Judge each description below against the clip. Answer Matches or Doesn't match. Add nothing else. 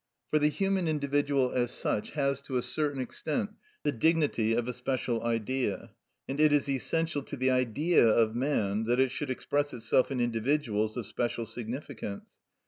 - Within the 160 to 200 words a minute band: Matches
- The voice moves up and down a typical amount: Matches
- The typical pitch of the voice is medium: Doesn't match